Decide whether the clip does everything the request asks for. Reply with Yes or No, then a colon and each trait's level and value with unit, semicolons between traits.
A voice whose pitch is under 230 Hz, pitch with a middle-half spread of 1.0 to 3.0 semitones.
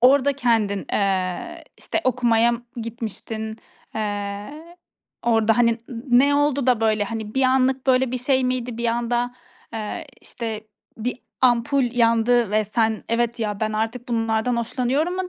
No: high, 235 Hz; narrow, 2.6 semitones